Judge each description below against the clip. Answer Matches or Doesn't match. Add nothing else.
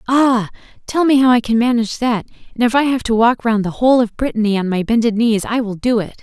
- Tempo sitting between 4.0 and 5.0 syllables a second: Doesn't match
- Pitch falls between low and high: Doesn't match